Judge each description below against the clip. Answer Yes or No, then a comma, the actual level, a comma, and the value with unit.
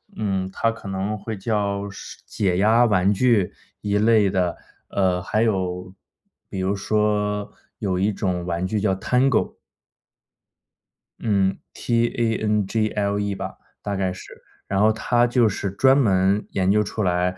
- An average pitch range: No, narrow, 2.3 semitones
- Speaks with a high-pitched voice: No, low, 100 Hz